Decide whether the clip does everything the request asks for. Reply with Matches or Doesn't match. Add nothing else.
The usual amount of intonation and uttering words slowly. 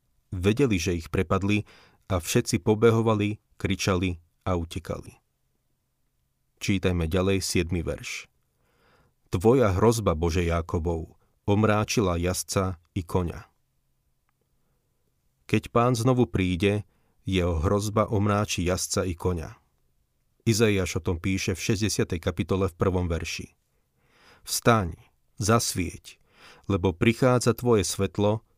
Matches